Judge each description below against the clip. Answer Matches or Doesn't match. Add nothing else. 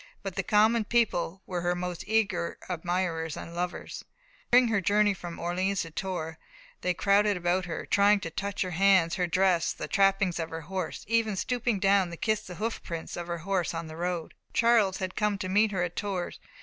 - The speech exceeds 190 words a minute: Matches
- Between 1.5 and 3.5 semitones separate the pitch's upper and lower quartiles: Matches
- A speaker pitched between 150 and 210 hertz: Matches